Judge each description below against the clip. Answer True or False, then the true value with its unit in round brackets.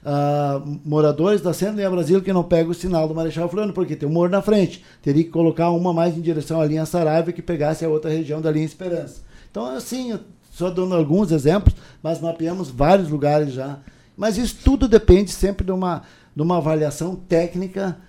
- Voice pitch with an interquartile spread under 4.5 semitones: True (2.9 semitones)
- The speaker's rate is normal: False (200 wpm)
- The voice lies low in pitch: False (170 Hz)